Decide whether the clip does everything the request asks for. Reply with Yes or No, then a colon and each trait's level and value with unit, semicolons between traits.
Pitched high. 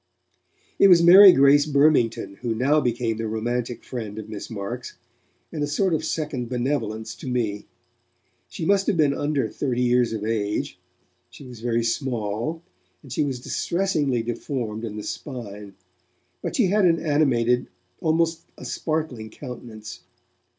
No: low, 125 Hz